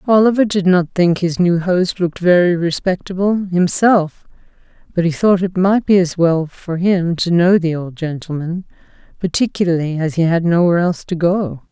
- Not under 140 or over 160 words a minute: No, average, 175 wpm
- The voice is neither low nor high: Yes, medium, 175 Hz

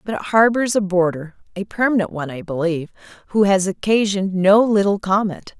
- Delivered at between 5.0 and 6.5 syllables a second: Yes, 5.7 syllables/s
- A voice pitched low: No, high, 195 Hz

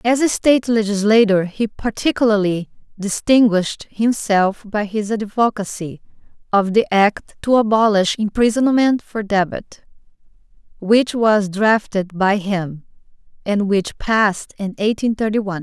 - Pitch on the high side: Yes, high, 210 Hz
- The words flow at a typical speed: No, slow, 120 wpm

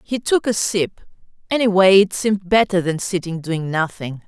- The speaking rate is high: No, average, 170 wpm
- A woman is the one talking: Yes, female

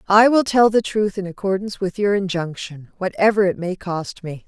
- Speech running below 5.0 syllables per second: No, 5.2 syllables/s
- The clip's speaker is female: Yes, female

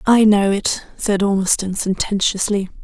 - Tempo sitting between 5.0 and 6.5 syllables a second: No, 4.4 syllables/s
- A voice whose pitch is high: Yes, high, 200 Hz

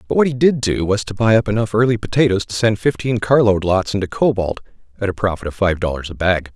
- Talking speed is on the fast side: Yes, fast, 245 wpm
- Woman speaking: No, male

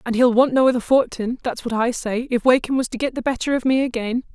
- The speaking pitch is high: Yes, high, 245 Hz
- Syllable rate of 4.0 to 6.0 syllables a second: No, 6.2 syllables/s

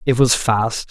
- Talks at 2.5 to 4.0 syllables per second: Yes, 3.8 syllables/s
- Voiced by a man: Yes, male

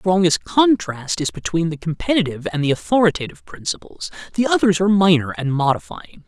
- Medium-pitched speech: Yes, medium, 175 Hz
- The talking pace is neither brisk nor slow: Yes, average, 160 wpm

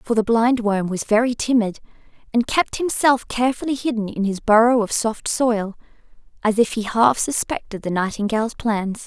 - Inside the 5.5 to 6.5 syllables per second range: No, 5.0 syllables/s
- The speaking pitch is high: Yes, high, 225 Hz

